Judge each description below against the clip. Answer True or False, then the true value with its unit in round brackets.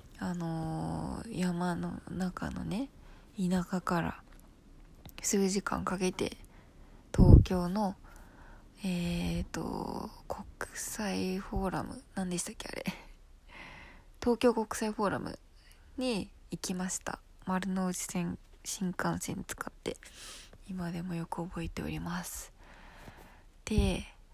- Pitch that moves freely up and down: False (2.5 semitones)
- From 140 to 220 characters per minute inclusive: True (190 characters per minute)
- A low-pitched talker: False (180 Hz)